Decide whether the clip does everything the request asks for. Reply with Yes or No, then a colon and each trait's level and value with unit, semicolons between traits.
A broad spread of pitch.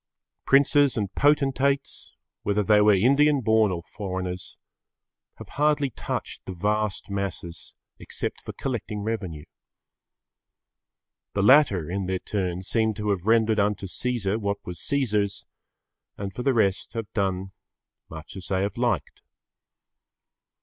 No: average, 3.8 semitones